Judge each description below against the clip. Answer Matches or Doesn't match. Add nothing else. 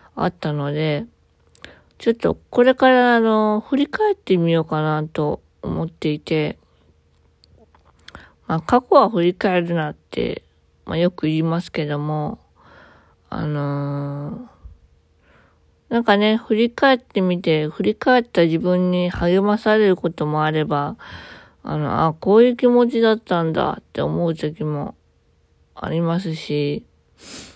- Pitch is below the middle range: Doesn't match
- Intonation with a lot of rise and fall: Matches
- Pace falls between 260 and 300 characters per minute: Doesn't match